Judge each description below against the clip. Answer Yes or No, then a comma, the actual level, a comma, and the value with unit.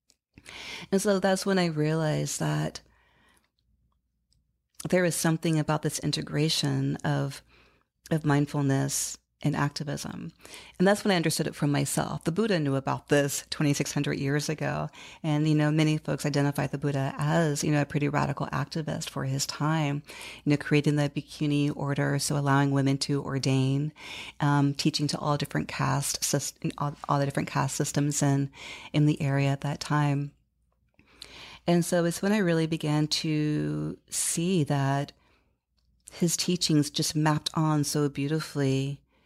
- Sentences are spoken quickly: No, average, 150 wpm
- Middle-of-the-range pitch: Yes, medium, 145 Hz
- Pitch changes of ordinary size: No, narrow, 2.0 semitones